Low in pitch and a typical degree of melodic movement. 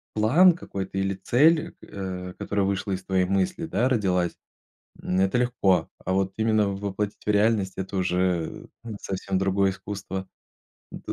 No: very low, 95 Hz; narrow, 2.1 semitones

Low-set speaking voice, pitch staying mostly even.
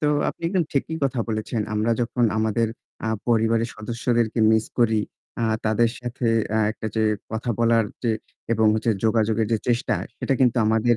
Yes: low, 115 Hz; narrow, 1.4 semitones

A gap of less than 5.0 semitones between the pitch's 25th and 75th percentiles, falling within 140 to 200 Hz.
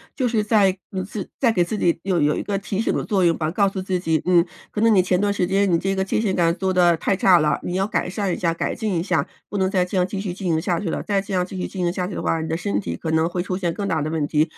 Yes: narrow, 2.6 semitones; medium, 185 Hz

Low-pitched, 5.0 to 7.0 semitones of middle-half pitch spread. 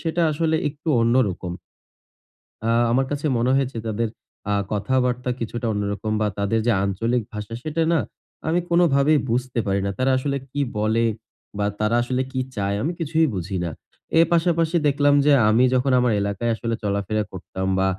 Yes: low, 120 Hz; wide, 5.4 semitones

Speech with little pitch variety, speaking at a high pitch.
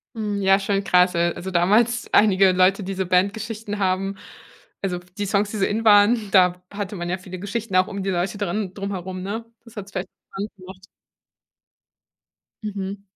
Yes: narrow, 1.9 semitones; high, 195 Hz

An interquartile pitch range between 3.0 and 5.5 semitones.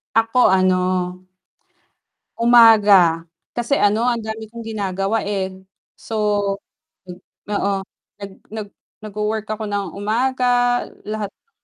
No: narrow, 2.5 semitones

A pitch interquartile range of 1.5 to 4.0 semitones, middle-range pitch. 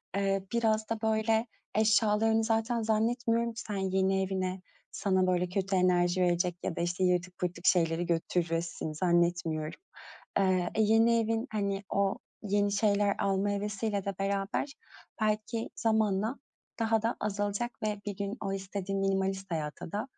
No: average, 2.9 semitones; high, 200 Hz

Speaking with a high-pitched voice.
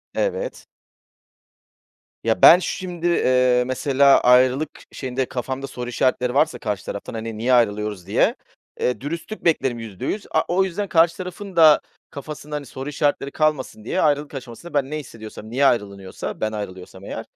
No: low, 135 Hz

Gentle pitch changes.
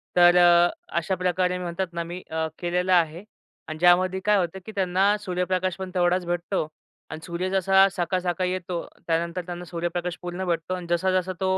Yes: narrow, 1.3 semitones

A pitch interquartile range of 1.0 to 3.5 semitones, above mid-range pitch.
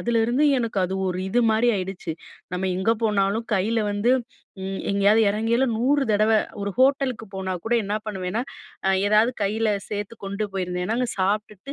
Yes: average, 3.0 semitones; high, 210 Hz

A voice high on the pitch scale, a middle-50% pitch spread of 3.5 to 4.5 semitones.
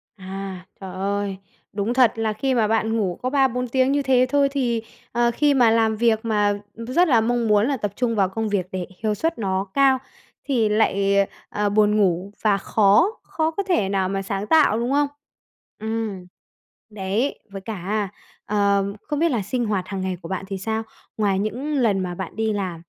Yes: high, 215 Hz; average, 4.0 semitones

